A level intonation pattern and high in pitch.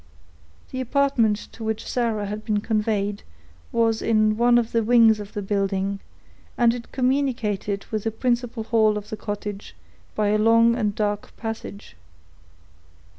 Yes: narrow, 2.0 semitones; high, 220 Hz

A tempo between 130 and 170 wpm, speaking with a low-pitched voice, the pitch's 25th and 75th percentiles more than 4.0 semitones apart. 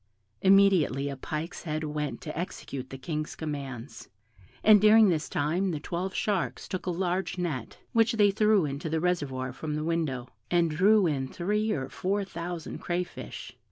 No: average, 165 wpm; medium, 170 Hz; average, 4.5 semitones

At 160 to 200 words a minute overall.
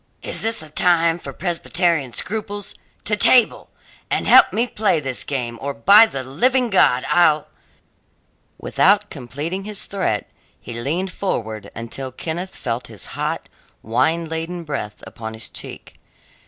No: average, 150 wpm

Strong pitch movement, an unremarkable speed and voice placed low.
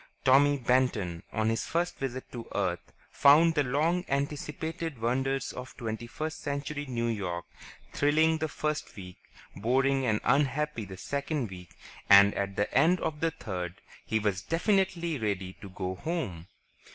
Yes: wide, 6.8 semitones; average, 150 wpm; low, 130 Hz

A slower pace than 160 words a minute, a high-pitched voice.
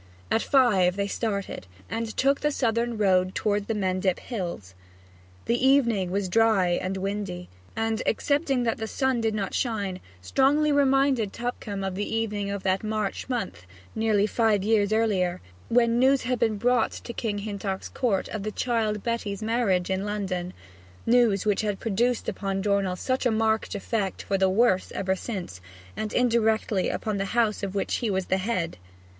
No: average, 170 wpm; high, 215 Hz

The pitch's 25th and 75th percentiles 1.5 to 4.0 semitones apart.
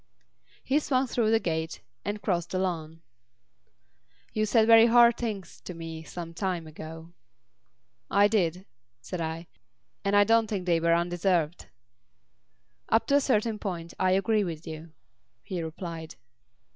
No: average, 4.6 semitones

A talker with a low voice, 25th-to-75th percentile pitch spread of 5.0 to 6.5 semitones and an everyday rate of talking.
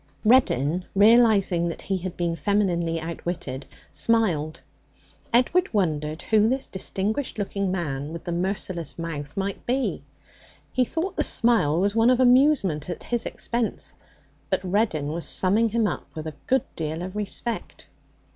No: high, 190 Hz; wide, 5.5 semitones; average, 145 wpm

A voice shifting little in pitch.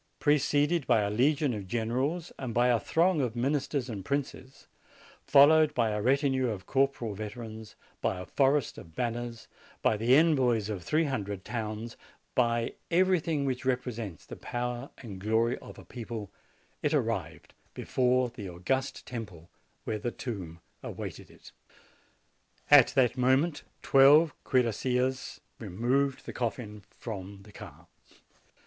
No: average, 4.0 semitones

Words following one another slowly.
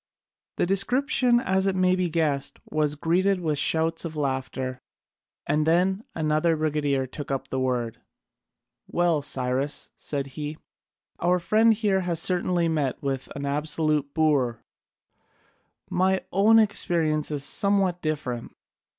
Yes: slow, 125 wpm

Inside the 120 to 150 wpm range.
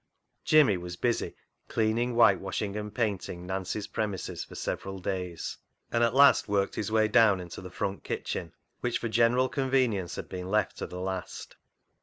No: average, 170 wpm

